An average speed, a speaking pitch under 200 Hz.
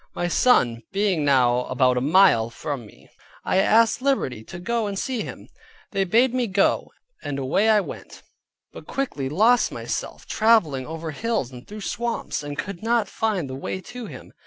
Yes: average, 180 wpm; high, 190 Hz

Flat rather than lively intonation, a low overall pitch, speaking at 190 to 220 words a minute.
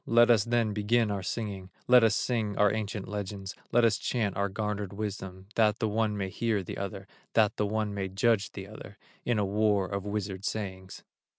Yes: narrow, 1.9 semitones; low, 105 Hz; average, 200 wpm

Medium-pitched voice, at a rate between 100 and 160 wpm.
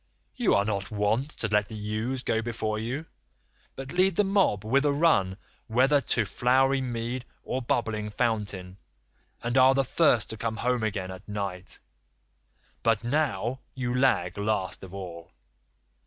No: low, 115 Hz; average, 155 wpm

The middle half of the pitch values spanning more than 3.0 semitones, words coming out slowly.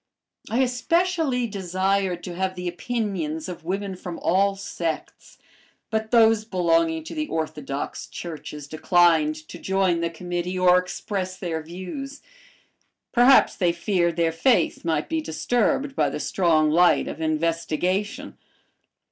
Yes: average, 3.9 semitones; slow, 130 wpm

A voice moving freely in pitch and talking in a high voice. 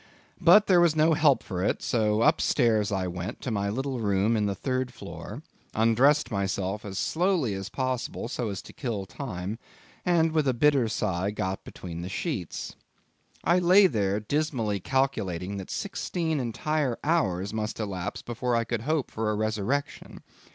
No: wide, 6.4 semitones; low, 115 Hz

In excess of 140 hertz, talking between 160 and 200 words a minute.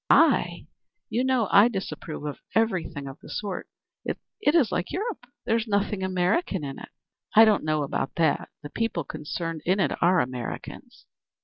Yes: high, 190 Hz; average, 165 wpm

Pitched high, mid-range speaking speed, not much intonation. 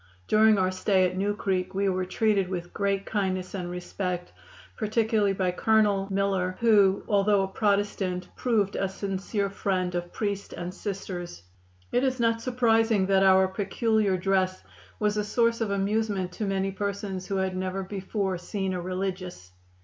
Yes: high, 195 Hz; average, 160 wpm; narrow, 1.9 semitones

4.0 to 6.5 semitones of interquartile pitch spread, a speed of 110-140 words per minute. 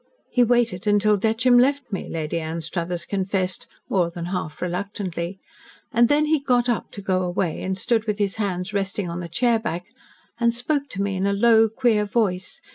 No: average, 4.4 semitones; average, 185 wpm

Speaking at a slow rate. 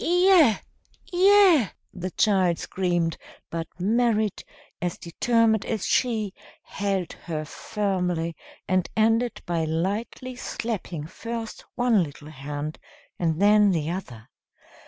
Yes: slow, 110 wpm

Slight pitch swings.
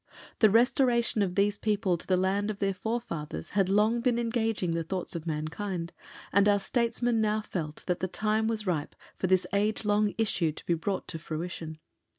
No: average, 3.8 semitones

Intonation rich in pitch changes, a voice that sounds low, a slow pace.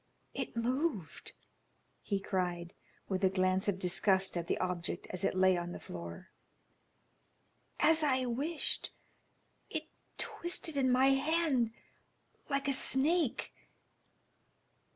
No: wide, 7.0 semitones; high, 220 Hz; slow, 115 wpm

